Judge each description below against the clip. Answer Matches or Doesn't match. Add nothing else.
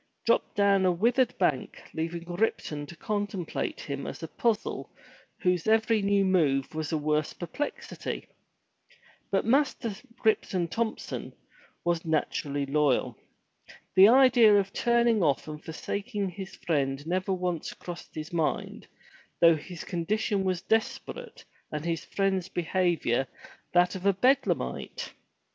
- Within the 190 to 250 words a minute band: Doesn't match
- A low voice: Doesn't match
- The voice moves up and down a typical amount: Matches